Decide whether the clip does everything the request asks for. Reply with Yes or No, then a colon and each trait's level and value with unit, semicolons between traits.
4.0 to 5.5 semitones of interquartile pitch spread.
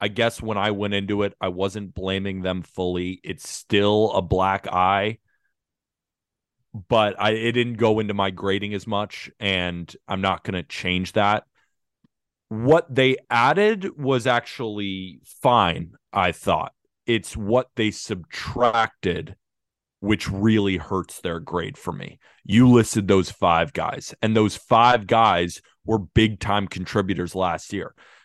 No: average, 2.9 semitones